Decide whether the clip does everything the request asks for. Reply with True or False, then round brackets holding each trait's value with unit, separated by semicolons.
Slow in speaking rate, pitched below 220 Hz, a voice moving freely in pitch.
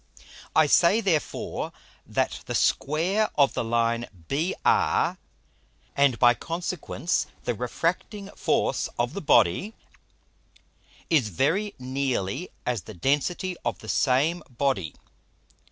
True (110 wpm; 140 Hz; 6.6 semitones)